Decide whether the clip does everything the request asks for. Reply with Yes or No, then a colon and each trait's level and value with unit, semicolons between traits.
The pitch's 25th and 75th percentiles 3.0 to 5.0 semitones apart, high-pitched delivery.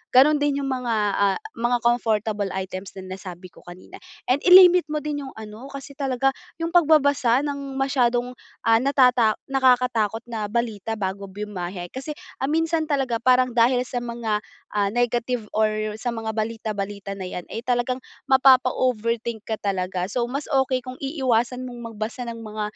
Yes: average, 3.6 semitones; high, 240 Hz